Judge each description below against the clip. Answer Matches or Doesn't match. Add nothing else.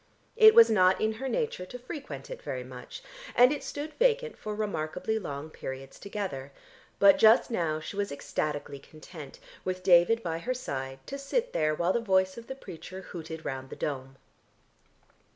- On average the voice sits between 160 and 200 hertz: Matches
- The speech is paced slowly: Doesn't match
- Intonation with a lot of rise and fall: Matches